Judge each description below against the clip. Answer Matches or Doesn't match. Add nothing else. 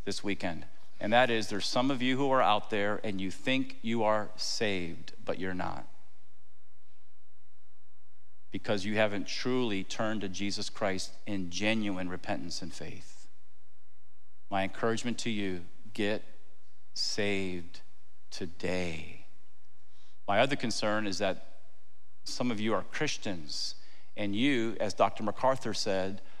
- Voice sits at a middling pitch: Doesn't match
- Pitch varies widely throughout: Doesn't match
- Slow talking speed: Matches